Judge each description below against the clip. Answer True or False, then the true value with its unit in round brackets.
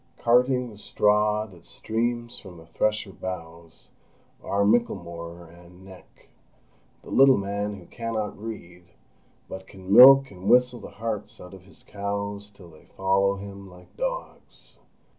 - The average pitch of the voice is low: True (100 Hz)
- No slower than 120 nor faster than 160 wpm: True (140 wpm)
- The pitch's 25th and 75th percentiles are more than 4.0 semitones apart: False (3.7 semitones)